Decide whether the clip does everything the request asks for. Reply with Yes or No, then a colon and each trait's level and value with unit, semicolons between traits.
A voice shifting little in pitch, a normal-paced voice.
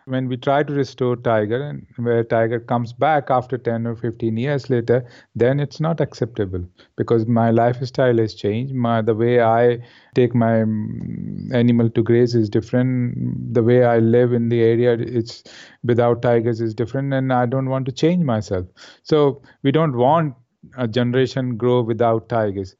Yes: narrow, 1.9 semitones; average, 170 wpm